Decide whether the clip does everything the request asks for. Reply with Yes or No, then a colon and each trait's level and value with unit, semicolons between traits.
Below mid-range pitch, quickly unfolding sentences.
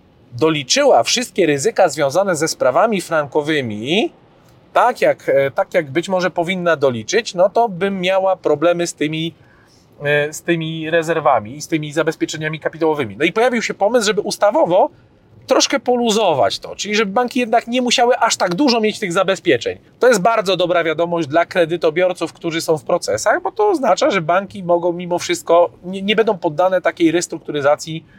No: medium, 175 Hz; fast, 165 wpm